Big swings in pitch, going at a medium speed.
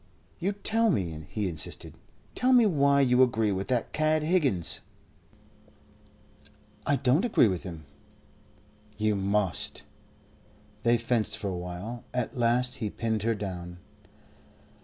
No: wide, 6.3 semitones; slow, 130 wpm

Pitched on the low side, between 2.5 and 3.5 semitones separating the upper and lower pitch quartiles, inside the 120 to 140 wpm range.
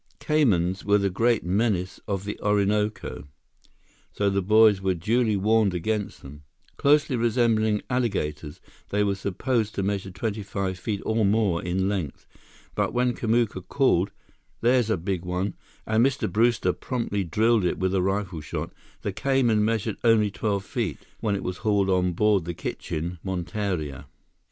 No: low, 100 Hz; average, 3.2 semitones; average, 155 wpm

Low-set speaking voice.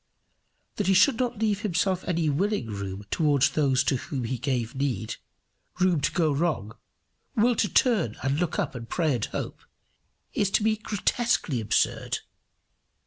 No: medium, 155 Hz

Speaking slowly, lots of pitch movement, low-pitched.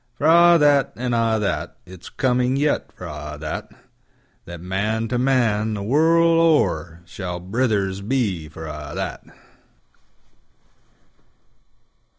Yes: slow, 110 wpm; wide, 6.9 semitones; low, 110 Hz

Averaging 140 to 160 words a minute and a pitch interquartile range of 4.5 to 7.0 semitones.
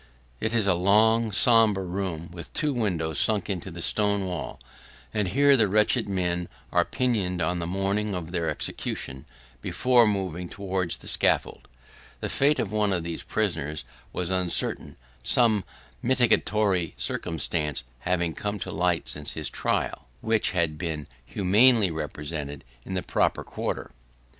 No: average, 150 wpm; average, 3.9 semitones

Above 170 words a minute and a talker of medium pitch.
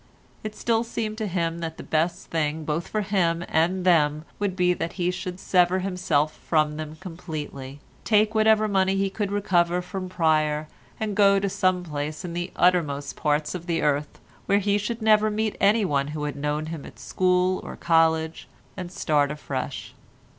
Yes: average, 180 wpm; medium, 175 Hz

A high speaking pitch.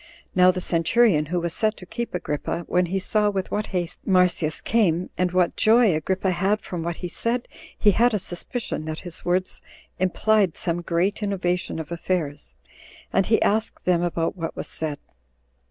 No: medium, 180 Hz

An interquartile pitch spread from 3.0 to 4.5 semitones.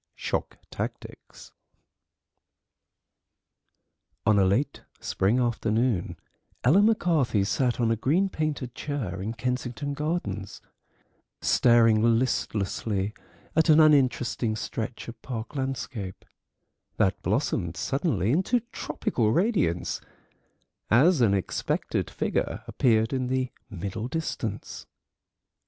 No: average, 4.9 semitones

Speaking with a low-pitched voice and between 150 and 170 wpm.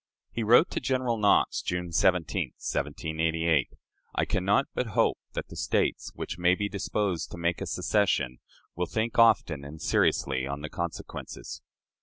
Yes: very low, 90 Hz; average, 160 wpm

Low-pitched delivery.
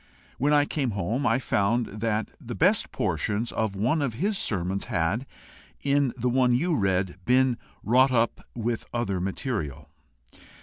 Yes: low, 120 Hz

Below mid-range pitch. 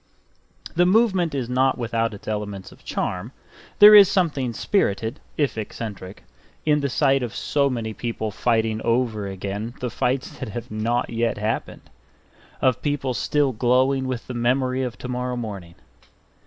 Yes: low, 120 Hz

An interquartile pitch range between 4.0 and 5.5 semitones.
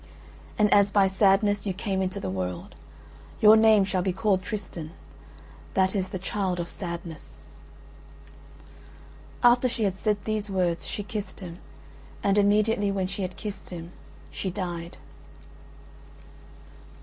No: narrow, 2.4 semitones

